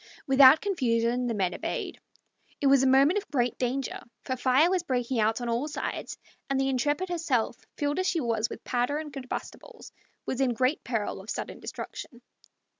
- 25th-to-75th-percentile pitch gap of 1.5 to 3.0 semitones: No, average, 3.4 semitones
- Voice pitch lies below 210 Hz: No, very high, 260 Hz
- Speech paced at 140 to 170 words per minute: No, average, 185 wpm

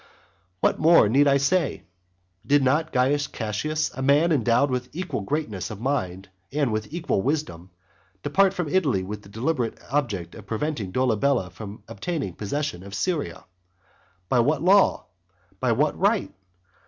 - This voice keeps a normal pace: Yes, average, 150 wpm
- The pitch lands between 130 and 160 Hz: Yes, low, 135 Hz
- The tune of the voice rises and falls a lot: Yes, wide, 6.3 semitones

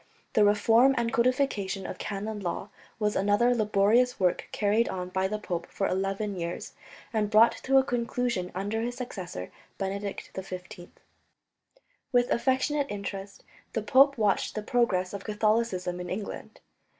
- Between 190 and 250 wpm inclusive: No, average, 145 wpm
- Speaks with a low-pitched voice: No, high, 210 Hz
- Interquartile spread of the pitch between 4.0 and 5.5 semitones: No, average, 3.5 semitones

